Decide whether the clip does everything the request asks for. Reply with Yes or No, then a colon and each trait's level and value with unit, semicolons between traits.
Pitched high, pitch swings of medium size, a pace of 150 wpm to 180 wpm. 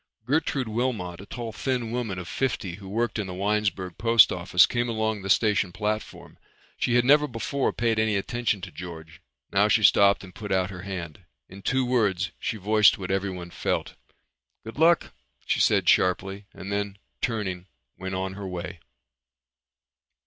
No: low, 100 Hz; average, 3.6 semitones; average, 170 wpm